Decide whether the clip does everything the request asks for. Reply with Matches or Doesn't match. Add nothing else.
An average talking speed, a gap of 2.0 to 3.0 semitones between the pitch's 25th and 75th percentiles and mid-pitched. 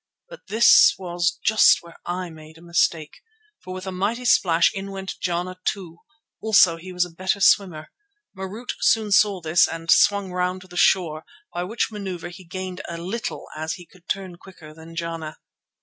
Matches